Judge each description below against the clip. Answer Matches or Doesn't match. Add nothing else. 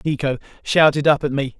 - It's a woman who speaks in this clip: Doesn't match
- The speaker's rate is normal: Matches